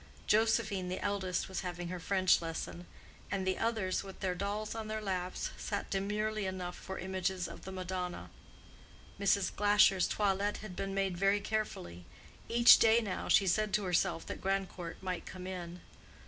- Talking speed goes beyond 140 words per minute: Yes, average, 160 wpm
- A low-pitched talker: No, high, 190 Hz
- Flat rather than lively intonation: Yes, narrow, 2.2 semitones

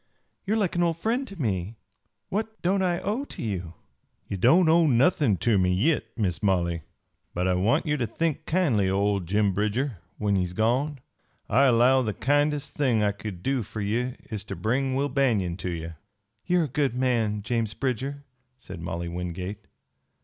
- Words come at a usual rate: Yes, average, 190 wpm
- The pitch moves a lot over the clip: Yes, wide, 6.8 semitones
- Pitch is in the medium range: No, low, 115 Hz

